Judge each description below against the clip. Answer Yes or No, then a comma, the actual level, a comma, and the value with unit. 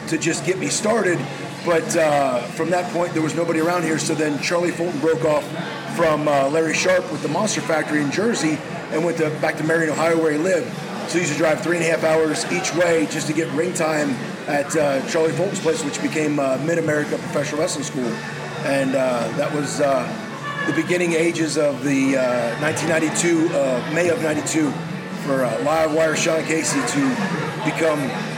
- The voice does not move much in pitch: Yes, narrow, 1.6 semitones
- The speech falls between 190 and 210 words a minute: Yes, average, 200 wpm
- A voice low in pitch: No, medium, 160 Hz